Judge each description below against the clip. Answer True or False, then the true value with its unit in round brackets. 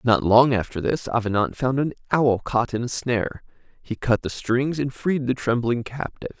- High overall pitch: False (120 Hz)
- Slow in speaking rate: False (195 wpm)